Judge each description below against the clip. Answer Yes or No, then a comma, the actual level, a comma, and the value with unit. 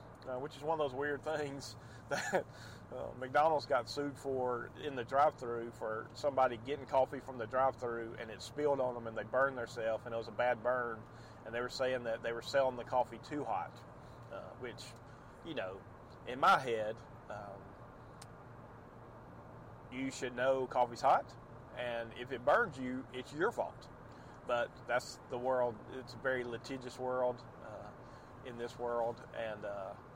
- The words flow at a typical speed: Yes, average, 175 wpm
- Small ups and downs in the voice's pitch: Yes, narrow, 2.0 semitones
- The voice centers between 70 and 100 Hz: No, low, 125 Hz